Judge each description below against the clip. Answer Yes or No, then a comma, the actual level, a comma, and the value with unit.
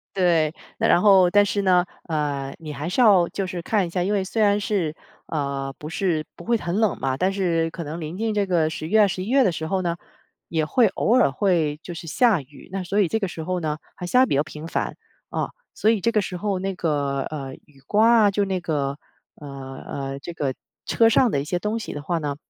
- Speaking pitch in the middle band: Yes, medium, 175 Hz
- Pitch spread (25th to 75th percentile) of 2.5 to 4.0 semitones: No, average, 4.8 semitones